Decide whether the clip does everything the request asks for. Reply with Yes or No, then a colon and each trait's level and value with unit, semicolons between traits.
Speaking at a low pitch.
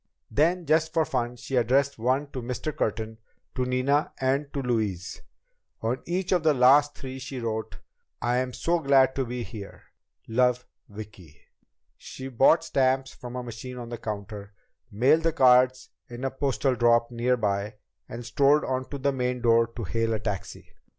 Yes: low, 125 Hz